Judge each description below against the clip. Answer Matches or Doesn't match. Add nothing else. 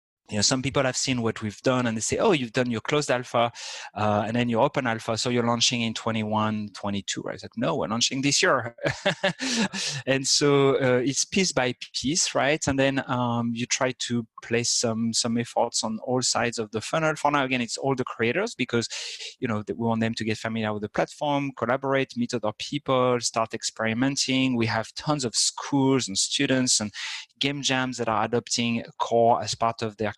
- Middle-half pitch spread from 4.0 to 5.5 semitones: Doesn't match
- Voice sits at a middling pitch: Doesn't match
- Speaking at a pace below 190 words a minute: Doesn't match